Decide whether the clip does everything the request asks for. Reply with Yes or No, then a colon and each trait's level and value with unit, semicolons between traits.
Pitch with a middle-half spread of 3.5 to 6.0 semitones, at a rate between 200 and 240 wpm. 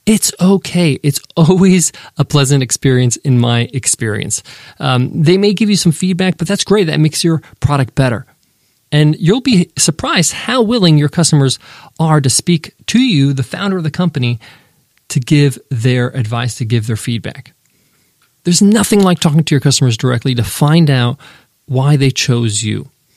No: average, 5.1 semitones; average, 170 wpm